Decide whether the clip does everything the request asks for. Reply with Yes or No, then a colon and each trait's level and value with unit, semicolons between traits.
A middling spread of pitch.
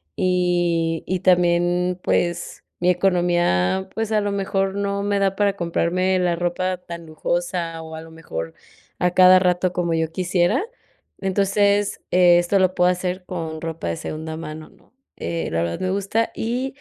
No: narrow, 2.2 semitones